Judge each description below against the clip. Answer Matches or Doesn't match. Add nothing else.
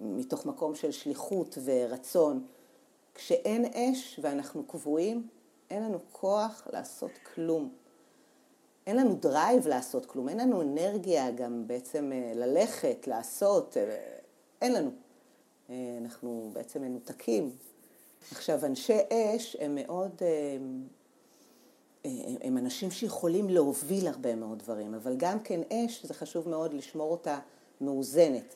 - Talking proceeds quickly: Doesn't match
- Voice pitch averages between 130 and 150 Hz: Doesn't match